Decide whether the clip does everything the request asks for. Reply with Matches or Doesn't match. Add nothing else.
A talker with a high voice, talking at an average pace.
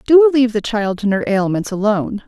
Doesn't match